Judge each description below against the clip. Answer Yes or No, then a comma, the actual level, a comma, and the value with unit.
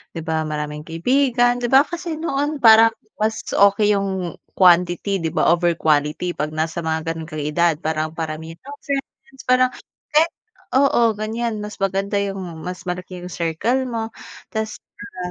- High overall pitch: Yes, high, 195 Hz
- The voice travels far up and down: Yes, wide, 6.7 semitones